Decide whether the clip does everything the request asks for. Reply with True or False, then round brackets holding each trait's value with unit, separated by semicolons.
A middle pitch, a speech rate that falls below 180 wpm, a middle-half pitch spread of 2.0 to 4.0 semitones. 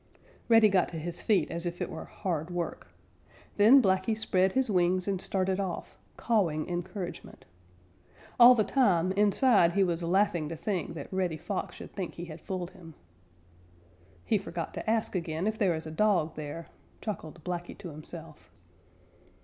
True (180 Hz; 165 wpm; 3.3 semitones)